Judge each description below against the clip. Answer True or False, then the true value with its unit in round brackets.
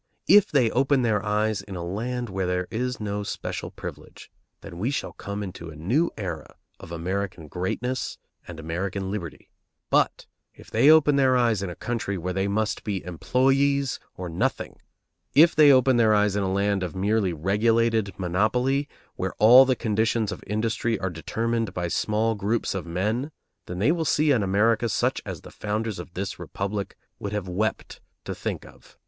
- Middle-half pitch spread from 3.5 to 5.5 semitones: True (4.2 semitones)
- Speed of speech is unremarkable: True (180 wpm)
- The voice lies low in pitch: True (105 Hz)